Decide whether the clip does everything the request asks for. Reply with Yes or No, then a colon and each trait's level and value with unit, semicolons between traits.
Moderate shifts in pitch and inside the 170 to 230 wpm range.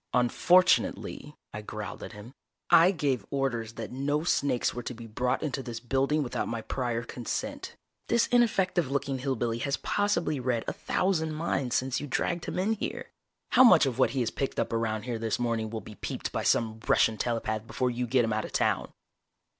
Yes: average, 4.4 semitones; average, 200 wpm